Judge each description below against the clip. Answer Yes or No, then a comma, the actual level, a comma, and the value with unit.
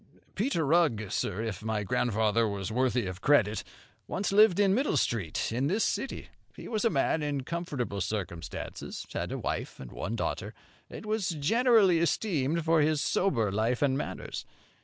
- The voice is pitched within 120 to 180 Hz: Yes, medium, 140 Hz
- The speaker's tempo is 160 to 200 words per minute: Yes, average, 165 wpm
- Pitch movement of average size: No, wide, 8.2 semitones